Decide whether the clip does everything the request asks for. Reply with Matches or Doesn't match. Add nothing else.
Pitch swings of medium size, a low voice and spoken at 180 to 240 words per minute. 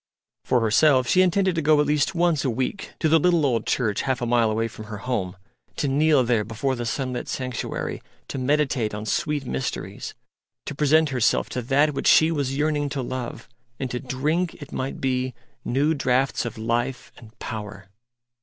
Matches